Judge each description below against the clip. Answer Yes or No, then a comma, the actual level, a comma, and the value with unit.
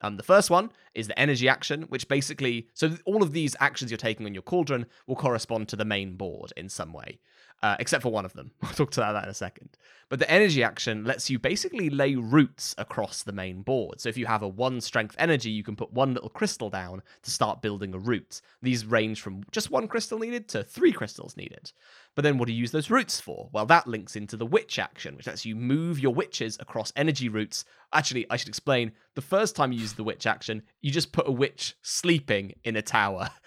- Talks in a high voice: No, low, 125 Hz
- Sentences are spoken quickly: Yes, fast, 240 wpm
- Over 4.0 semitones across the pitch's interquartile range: Yes, average, 5.3 semitones